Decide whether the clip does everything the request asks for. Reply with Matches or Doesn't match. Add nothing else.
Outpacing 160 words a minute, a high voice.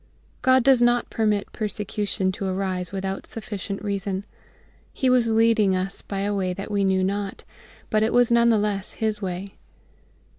Matches